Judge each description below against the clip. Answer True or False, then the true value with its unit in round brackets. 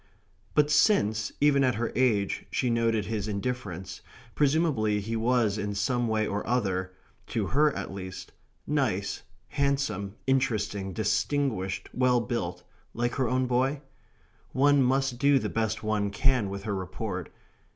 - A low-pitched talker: True (115 Hz)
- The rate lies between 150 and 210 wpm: False (140 wpm)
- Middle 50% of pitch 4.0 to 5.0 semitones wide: True (4.6 semitones)